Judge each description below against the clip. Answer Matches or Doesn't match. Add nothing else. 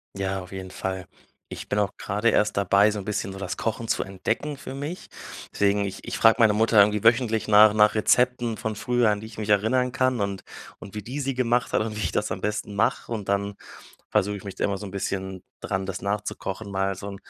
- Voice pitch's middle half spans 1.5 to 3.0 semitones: Matches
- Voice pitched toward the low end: Matches